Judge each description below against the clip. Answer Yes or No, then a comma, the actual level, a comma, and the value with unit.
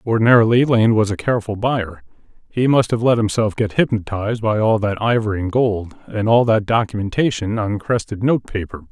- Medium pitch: No, low, 110 Hz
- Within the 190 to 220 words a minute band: No, average, 175 wpm